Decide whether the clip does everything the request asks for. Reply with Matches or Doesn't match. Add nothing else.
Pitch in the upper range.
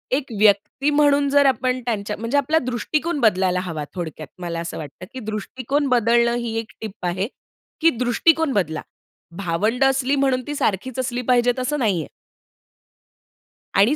Matches